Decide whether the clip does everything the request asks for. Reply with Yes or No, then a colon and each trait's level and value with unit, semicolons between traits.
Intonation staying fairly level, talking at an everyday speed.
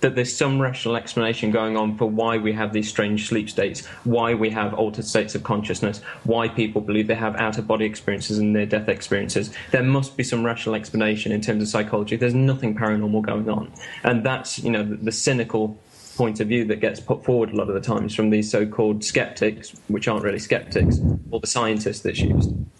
No: narrow, 1.6 semitones; fast, 215 wpm